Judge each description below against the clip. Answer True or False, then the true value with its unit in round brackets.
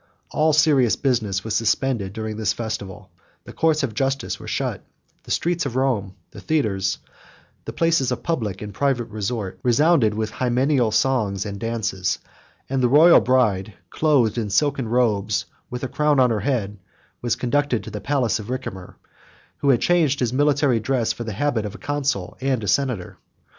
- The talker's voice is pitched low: True (120 Hz)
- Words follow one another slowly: False (175 wpm)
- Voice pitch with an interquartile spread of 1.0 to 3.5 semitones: False (4.6 semitones)